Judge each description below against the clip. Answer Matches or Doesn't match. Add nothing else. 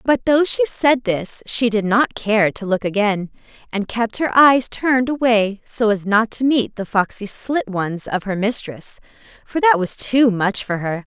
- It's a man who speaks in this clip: Doesn't match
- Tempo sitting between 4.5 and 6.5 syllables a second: Doesn't match